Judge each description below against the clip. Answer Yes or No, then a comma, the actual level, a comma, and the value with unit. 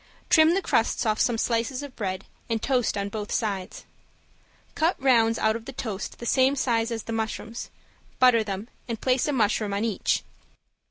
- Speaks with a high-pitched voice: Yes, high, 230 Hz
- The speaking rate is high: No, average, 180 wpm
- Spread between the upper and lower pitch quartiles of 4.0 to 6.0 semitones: No, average, 2.9 semitones